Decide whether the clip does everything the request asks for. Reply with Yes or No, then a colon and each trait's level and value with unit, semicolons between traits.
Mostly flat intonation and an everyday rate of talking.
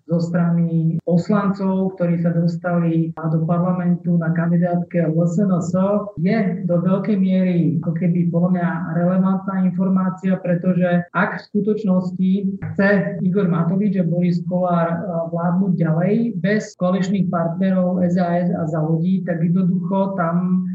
Yes: narrow, 1.8 semitones; average, 130 wpm